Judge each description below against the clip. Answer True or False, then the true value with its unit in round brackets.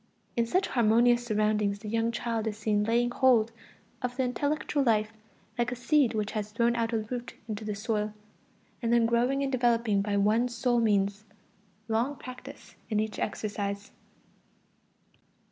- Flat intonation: True (2.2 semitones)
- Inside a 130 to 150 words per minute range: False (160 wpm)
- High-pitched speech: True (230 Hz)